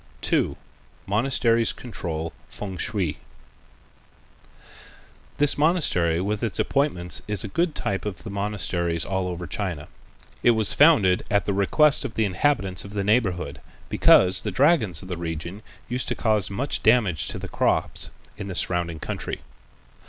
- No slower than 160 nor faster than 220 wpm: No, average, 150 wpm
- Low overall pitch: Yes, low, 100 Hz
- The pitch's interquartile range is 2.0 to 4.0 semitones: No, average, 4.5 semitones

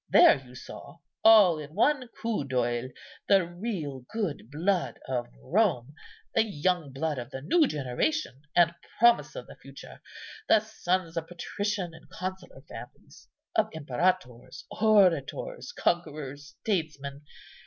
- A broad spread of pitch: Yes, wide, 6.6 semitones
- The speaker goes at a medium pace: No, slow, 130 wpm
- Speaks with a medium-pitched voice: Yes, medium, 170 Hz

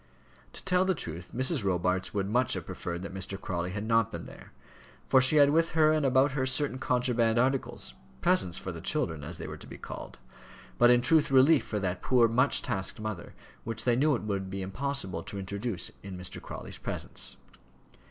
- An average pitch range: No, wide, 6.0 semitones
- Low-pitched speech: Yes, low, 115 Hz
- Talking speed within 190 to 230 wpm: Yes, average, 200 wpm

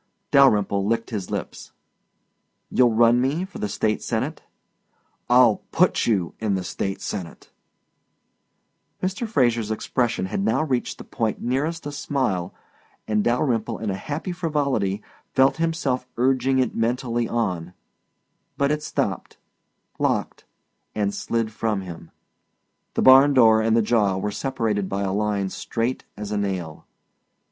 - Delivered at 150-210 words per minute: No, average, 140 wpm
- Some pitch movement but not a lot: Yes, average, 4.4 semitones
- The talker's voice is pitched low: Yes, low, 115 Hz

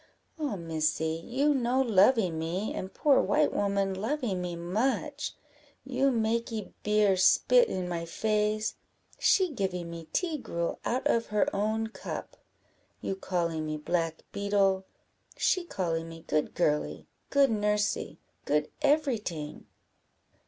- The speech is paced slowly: Yes, slow, 130 wpm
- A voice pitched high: Yes, high, 205 Hz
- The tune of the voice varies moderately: No, wide, 6.2 semitones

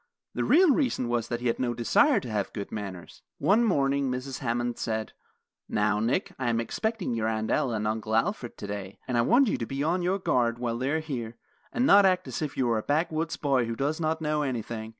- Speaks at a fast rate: Yes, fast, 230 wpm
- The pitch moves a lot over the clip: Yes, wide, 5.7 semitones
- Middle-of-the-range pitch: No, low, 125 Hz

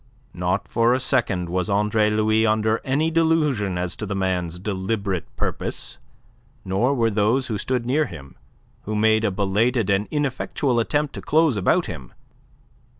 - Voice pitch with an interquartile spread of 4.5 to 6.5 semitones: Yes, average, 4.8 semitones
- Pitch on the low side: Yes, low, 110 Hz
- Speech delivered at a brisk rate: No, average, 155 wpm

